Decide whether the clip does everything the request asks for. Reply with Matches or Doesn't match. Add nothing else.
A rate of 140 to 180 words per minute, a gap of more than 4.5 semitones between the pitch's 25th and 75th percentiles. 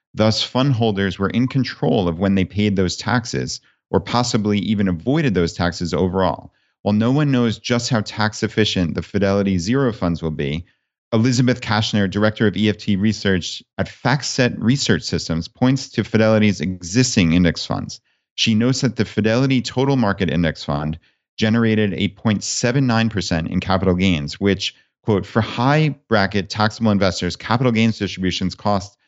Doesn't match